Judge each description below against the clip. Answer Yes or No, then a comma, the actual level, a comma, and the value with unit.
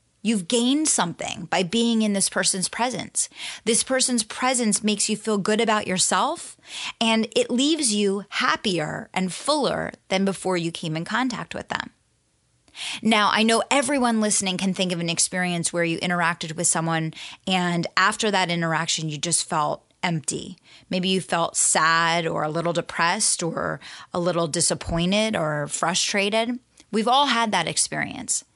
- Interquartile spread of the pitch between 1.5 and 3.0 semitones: No, average, 4.8 semitones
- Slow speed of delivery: No, average, 160 wpm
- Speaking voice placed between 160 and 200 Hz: Yes, high, 190 Hz